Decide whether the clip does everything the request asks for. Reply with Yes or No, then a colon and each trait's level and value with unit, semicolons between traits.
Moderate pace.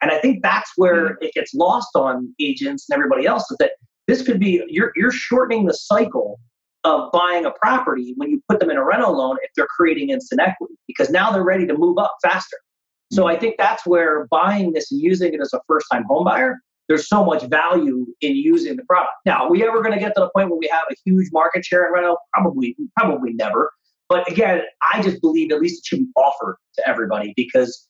No: fast, 230 wpm